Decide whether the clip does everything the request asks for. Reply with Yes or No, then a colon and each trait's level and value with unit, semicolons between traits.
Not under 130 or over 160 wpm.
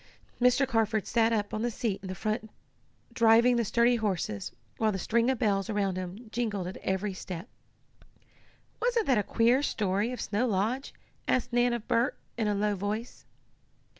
No: average, 170 wpm